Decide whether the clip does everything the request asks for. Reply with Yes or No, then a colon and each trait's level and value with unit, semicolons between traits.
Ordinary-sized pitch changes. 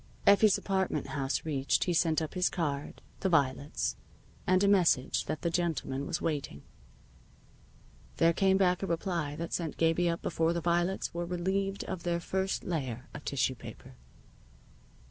Yes: average, 3.6 semitones